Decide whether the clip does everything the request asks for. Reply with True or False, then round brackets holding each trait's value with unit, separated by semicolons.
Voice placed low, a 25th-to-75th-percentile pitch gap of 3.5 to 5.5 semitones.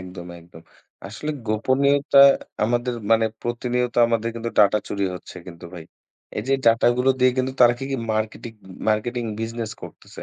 False (115 Hz; 2.6 semitones)